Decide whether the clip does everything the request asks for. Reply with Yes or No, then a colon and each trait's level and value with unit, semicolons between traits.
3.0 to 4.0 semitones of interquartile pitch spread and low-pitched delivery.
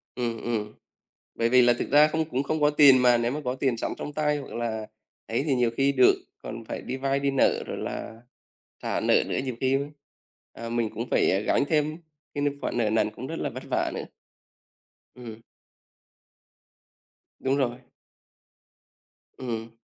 Yes: average, 3.3 semitones; low, 130 Hz